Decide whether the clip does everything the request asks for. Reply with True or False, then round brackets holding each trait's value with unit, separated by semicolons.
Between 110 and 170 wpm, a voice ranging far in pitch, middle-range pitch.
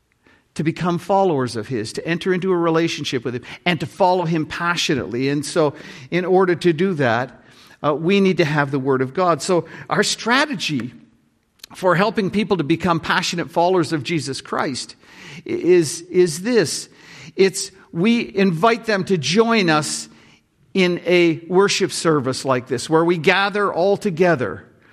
False (160 wpm; 4.2 semitones; 175 Hz)